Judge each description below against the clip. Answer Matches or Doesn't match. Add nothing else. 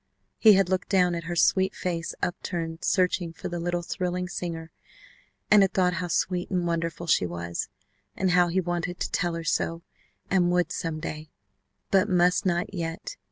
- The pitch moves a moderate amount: Doesn't match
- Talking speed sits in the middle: Matches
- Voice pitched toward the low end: Doesn't match